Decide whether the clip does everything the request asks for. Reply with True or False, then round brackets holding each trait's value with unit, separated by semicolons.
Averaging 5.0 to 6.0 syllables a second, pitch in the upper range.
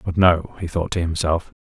False (5.1 syllables/s; 85 Hz)